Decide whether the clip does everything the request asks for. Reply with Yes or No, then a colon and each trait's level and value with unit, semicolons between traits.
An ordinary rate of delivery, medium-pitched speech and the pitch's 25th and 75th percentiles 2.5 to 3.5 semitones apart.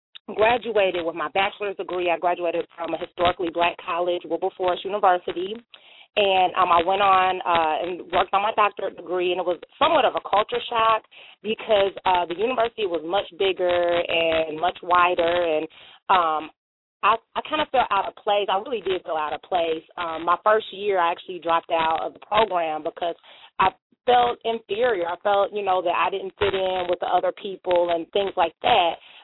Yes: average, 190 wpm; medium, 180 Hz; average, 3.0 semitones